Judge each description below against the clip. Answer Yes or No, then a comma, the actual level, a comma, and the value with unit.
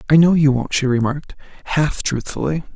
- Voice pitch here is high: No, medium, 145 Hz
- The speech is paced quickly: No, average, 175 wpm